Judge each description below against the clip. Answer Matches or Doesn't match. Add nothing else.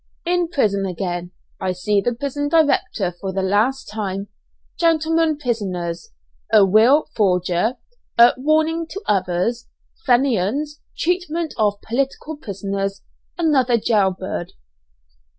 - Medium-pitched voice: Doesn't match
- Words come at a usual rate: Doesn't match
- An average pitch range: Doesn't match